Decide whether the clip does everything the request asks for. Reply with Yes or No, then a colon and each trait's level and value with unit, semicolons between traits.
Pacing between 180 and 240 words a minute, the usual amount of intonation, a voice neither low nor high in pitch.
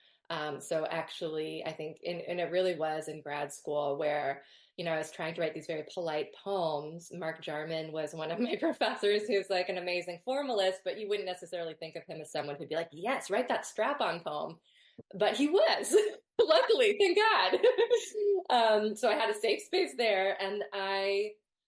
No: average, 195 wpm; wide, 5.7 semitones; medium, 180 Hz